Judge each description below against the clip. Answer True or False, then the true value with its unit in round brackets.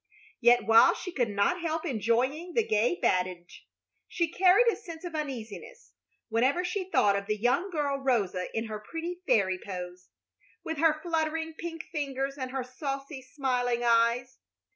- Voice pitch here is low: False (270 Hz)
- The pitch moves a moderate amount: False (6.3 semitones)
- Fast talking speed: False (160 wpm)